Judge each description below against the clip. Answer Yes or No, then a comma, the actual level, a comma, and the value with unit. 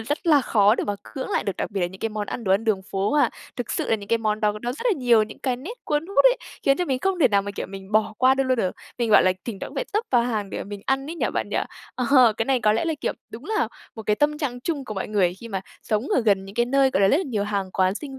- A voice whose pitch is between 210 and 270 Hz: Yes, high, 225 Hz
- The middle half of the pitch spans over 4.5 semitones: Yes, average, 4.9 semitones